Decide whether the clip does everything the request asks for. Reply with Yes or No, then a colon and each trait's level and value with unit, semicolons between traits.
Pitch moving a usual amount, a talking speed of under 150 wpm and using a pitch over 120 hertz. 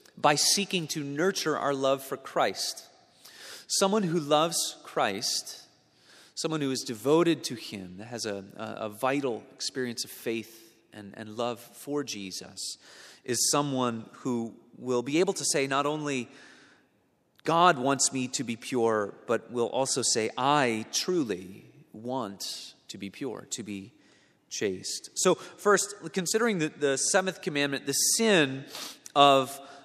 Yes: average, 4.9 semitones; average, 140 wpm; low, 135 Hz